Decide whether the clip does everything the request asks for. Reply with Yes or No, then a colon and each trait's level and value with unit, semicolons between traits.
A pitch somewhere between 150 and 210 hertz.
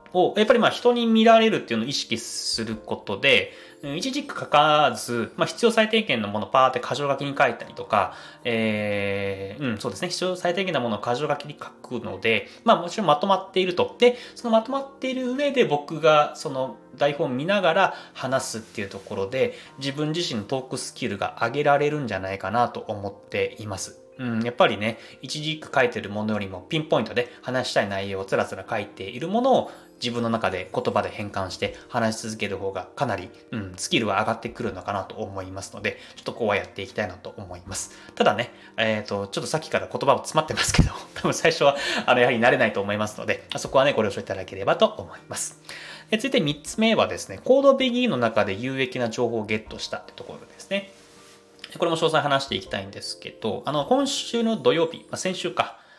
No: low, 135 Hz